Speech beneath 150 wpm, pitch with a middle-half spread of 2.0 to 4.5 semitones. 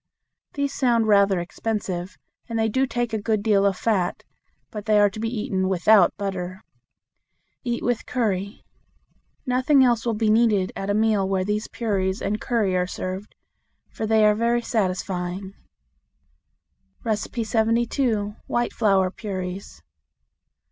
Yes: average, 140 wpm; average, 3.1 semitones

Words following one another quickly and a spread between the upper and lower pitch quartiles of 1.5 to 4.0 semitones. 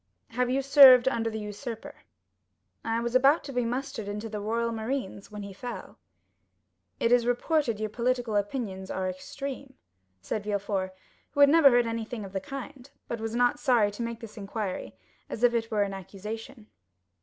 No: average, 180 wpm; average, 3.3 semitones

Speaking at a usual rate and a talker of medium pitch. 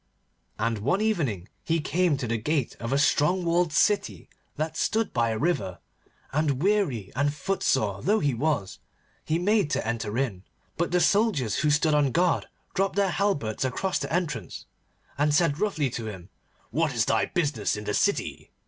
Yes: average, 175 wpm; medium, 150 Hz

